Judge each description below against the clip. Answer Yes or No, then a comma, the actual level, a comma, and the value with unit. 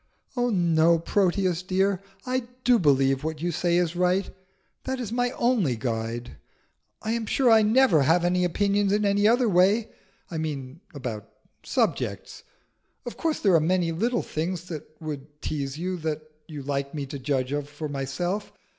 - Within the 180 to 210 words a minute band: No, average, 170 wpm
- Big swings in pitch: Yes, wide, 5.7 semitones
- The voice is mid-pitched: Yes, medium, 175 Hz